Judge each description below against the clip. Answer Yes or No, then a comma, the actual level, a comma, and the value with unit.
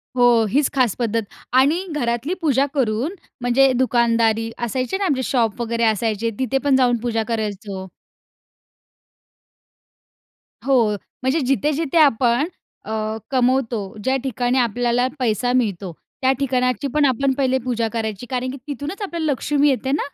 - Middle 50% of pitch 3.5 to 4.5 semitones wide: No, average, 3.0 semitones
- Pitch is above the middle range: Yes, very high, 250 Hz